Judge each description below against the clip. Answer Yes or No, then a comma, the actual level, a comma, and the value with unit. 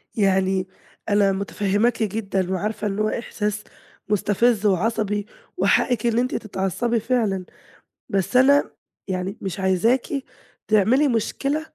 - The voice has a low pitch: No, high, 210 Hz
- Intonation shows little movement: No, average, 3.3 semitones